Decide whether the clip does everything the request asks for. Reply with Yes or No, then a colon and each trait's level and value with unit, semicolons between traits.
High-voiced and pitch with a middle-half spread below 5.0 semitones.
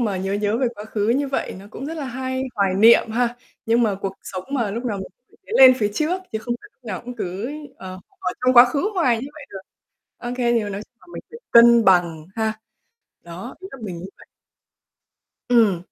Yes: high, 230 Hz; average, 4.3 semitones